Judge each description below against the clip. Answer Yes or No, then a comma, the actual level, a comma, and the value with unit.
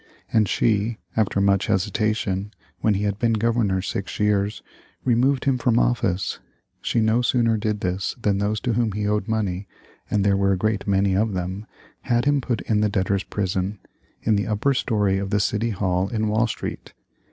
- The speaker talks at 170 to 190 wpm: Yes, average, 185 wpm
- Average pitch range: No, narrow, 2.3 semitones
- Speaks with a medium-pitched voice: No, low, 105 Hz